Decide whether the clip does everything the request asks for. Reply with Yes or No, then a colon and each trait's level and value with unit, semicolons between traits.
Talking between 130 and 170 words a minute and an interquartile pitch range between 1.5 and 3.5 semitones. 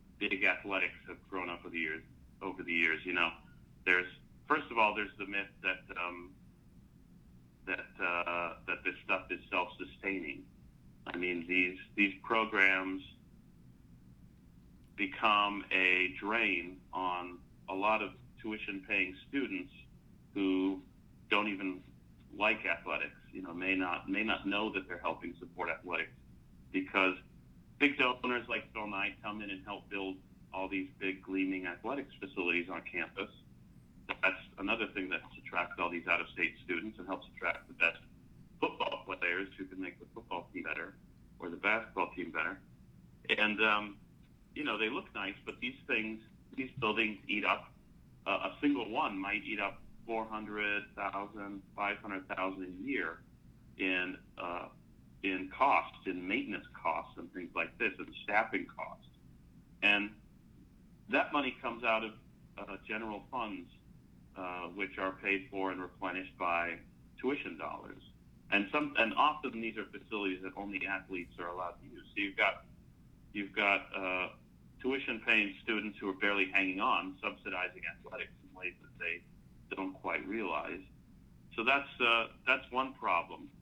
Yes: average, 150 wpm; narrow, 2.5 semitones